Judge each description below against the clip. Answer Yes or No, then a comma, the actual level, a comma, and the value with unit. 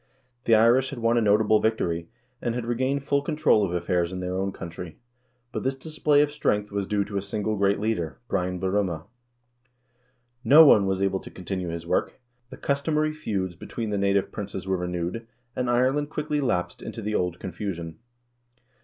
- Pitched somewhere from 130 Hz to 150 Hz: No, low, 105 Hz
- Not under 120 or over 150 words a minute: No, average, 190 wpm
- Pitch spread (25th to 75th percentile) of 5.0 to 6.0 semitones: Yes, wide, 5.4 semitones